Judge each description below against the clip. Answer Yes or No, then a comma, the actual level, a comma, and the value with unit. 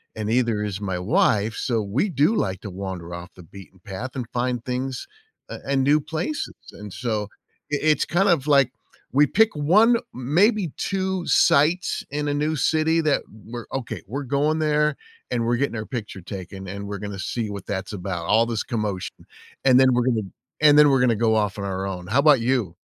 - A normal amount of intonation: No, wide, 6.4 semitones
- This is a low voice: Yes, low, 120 Hz